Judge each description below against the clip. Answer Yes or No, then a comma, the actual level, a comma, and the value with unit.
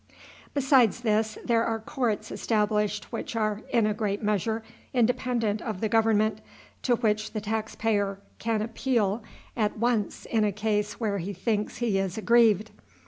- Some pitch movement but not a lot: No, narrow, 1.6 semitones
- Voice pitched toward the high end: Yes, high, 220 Hz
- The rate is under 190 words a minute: Yes, average, 155 wpm